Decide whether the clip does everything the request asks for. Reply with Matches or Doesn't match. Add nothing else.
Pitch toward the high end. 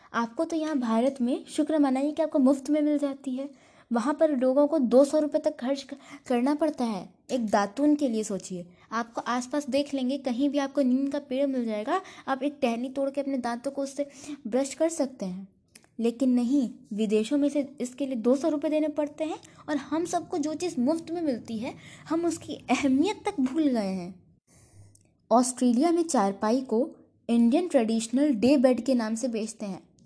Matches